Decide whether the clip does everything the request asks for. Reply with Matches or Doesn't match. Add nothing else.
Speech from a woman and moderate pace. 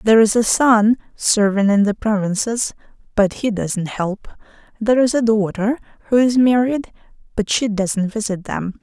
Matches